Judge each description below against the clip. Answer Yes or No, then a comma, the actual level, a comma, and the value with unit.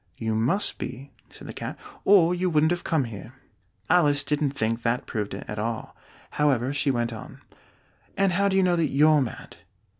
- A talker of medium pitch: Yes, medium, 145 Hz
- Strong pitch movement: Yes, wide, 6.4 semitones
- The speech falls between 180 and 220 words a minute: Yes, average, 190 wpm